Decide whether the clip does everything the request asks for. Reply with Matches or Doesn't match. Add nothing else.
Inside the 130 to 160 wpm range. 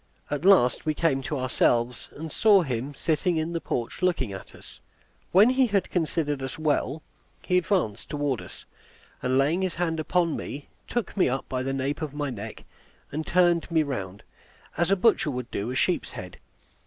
Doesn't match